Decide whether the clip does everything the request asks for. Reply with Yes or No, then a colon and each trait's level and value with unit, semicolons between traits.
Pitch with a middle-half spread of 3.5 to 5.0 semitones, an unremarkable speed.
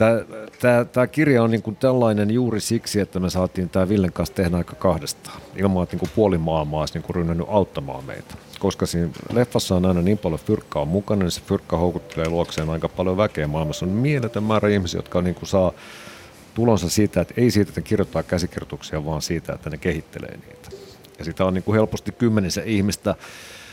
No: average, 3.8 semitones; fast, 195 wpm